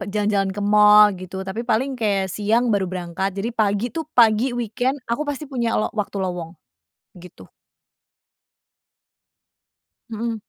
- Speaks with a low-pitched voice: No, high, 210 Hz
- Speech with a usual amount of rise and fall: Yes, average, 3.3 semitones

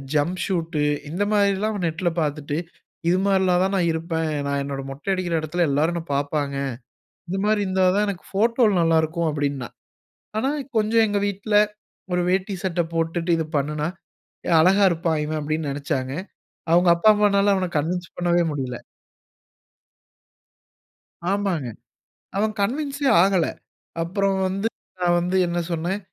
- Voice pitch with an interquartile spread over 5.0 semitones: No, average, 3.9 semitones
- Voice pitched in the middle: Yes, medium, 175 Hz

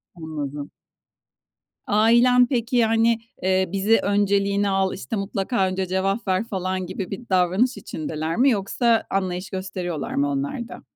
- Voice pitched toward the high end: Yes, high, 195 Hz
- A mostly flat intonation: No, average, 3.3 semitones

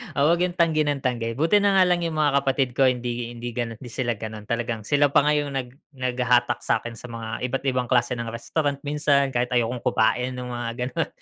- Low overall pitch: Yes, low, 125 Hz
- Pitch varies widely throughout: No, average, 3.3 semitones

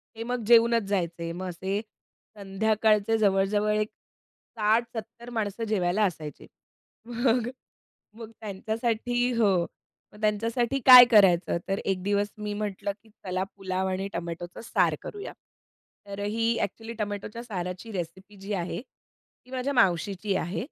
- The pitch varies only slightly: No, average, 3.1 semitones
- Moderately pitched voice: No, high, 210 Hz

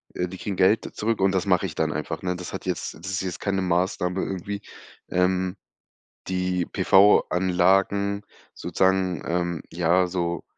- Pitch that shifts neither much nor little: No, narrow, 1.4 semitones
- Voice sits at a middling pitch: No, very low, 90 Hz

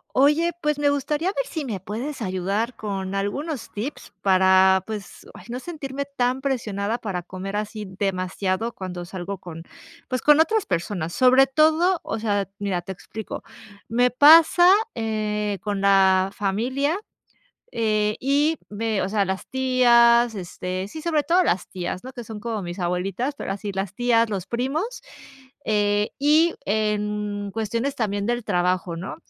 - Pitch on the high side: Yes, high, 215 Hz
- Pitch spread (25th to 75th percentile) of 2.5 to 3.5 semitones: No, average, 5.2 semitones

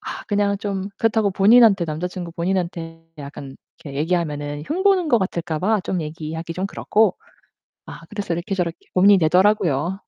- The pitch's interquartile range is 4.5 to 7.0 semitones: No, average, 3.8 semitones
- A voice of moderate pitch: Yes, medium, 180 Hz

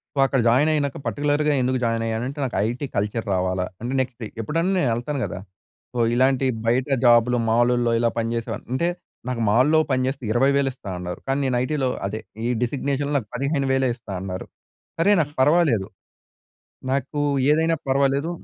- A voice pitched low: Yes, low, 130 Hz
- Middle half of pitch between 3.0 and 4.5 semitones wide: Yes, average, 3.3 semitones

